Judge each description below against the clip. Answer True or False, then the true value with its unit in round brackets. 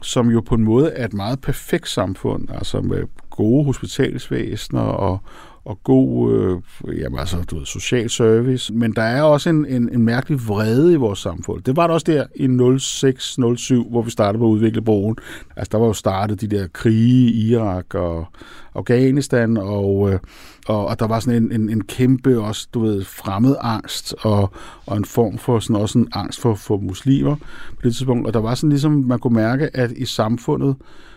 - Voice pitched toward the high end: False (115 Hz)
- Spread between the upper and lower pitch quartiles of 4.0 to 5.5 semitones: False (3.6 semitones)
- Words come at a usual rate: True (200 wpm)